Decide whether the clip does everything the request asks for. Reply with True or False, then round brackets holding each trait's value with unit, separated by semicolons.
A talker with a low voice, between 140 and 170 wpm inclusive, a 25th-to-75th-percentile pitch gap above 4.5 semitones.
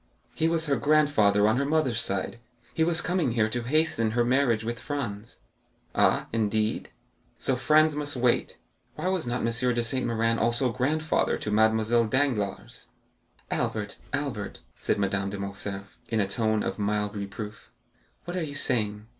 True (115 Hz; 165 wpm; 5.1 semitones)